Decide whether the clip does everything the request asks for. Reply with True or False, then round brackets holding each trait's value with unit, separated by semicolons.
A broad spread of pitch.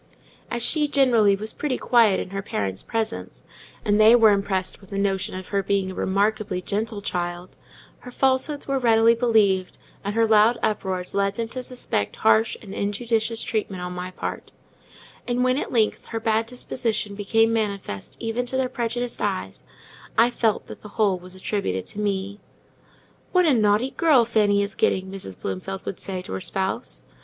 False (3.3 semitones)